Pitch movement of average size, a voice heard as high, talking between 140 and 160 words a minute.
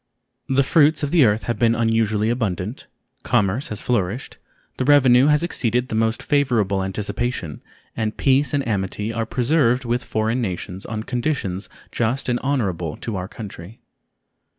No: average, 3.8 semitones; low, 115 Hz; average, 150 wpm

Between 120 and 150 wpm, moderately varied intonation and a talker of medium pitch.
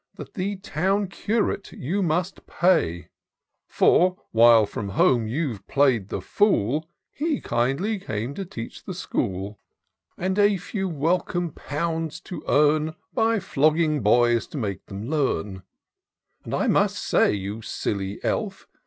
No: slow, 135 wpm; wide, 8.5 semitones; medium, 150 Hz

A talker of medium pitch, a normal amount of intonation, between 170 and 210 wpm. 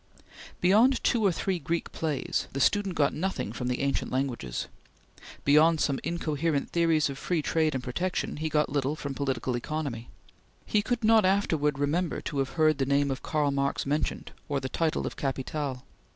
Yes: medium, 150 Hz; average, 3.6 semitones; average, 180 wpm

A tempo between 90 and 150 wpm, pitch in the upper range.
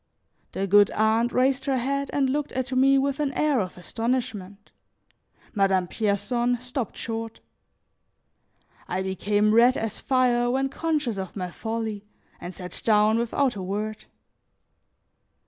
Yes: slow, 135 wpm; high, 230 Hz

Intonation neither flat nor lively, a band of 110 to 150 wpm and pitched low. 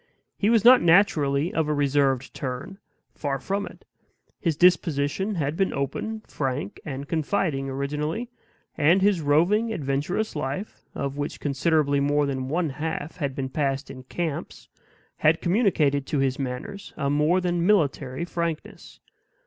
No: average, 4.4 semitones; average, 145 wpm; medium, 150 Hz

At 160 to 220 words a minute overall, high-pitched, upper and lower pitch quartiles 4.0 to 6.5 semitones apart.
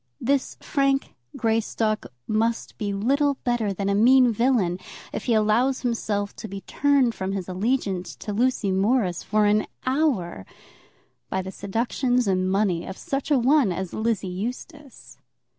No: average, 150 wpm; high, 220 Hz; average, 4.6 semitones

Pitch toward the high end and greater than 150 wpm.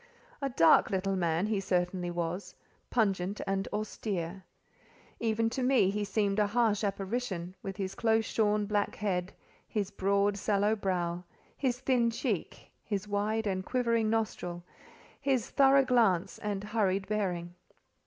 No: high, 205 Hz; average, 140 wpm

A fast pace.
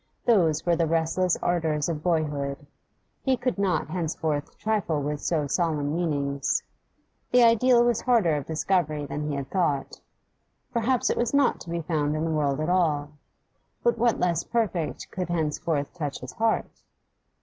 No: average, 160 wpm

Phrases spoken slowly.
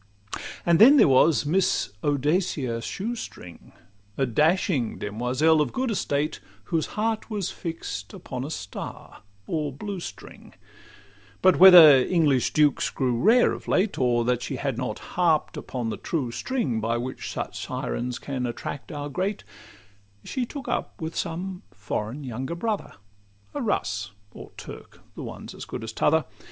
No: average, 155 wpm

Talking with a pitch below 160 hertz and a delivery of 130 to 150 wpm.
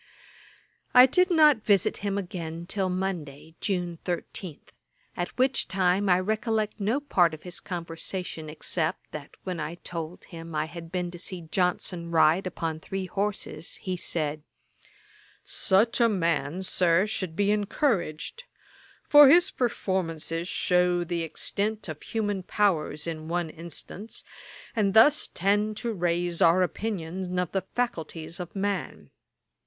No: medium, 180 Hz; average, 140 wpm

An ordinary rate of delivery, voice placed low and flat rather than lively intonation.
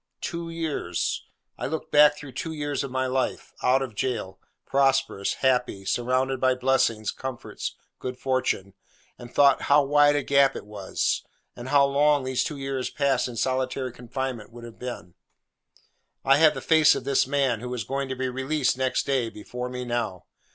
Yes: average, 175 wpm; low, 130 Hz; narrow, 2.1 semitones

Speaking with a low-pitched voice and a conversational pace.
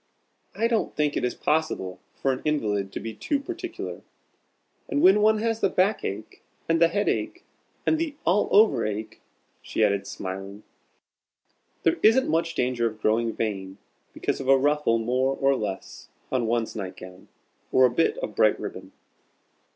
Yes: low, 130 Hz; average, 170 wpm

